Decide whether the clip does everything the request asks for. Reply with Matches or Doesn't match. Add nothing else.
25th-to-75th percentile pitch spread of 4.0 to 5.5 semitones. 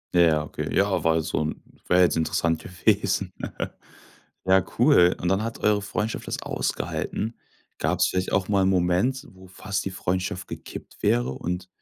Doesn't match